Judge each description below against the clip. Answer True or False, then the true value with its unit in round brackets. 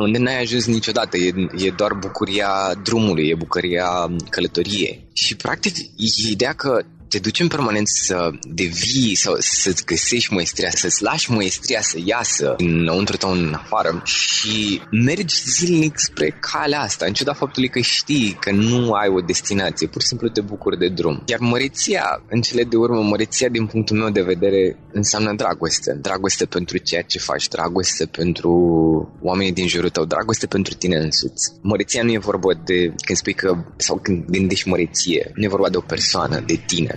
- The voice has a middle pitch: False (105 Hz)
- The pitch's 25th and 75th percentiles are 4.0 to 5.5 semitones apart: True (4.3 semitones)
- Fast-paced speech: True (175 wpm)